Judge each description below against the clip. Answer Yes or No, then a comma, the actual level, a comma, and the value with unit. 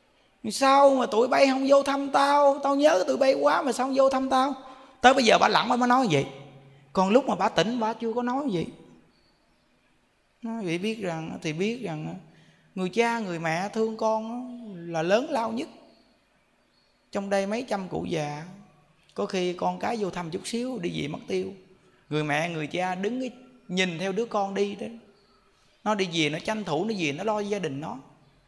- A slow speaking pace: No, average, 210 wpm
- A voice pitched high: Yes, high, 210 Hz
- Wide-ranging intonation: Yes, wide, 6.1 semitones